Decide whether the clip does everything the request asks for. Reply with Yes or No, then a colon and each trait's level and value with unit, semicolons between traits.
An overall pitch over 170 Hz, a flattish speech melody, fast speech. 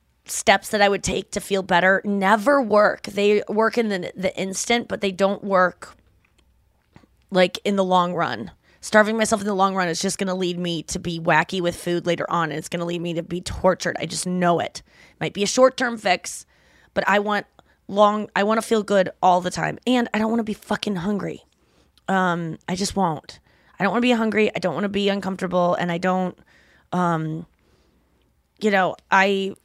No: high, 190 Hz; average, 3.1 semitones; fast, 215 wpm